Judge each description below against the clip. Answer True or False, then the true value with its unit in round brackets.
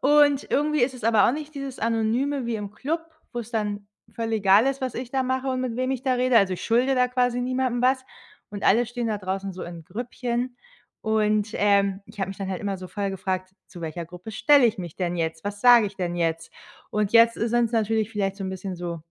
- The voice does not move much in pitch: False (4.5 semitones)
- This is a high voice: True (220 Hz)